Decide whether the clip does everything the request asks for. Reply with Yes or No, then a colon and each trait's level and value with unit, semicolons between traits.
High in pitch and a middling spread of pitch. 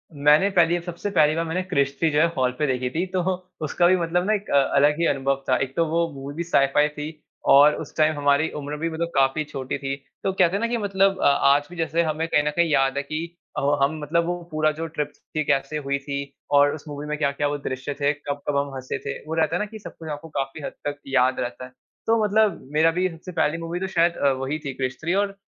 No: medium, 150 Hz; average, 3.3 semitones